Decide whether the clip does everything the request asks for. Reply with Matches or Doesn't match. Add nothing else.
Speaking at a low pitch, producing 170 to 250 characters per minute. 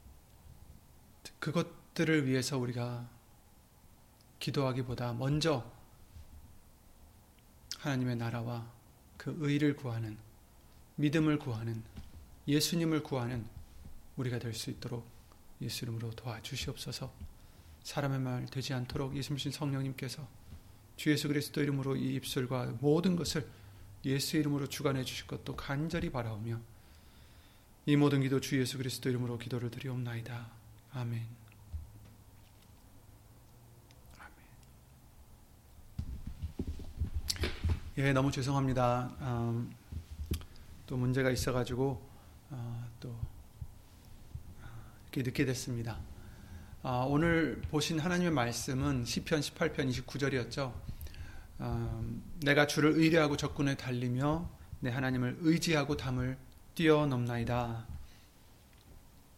Matches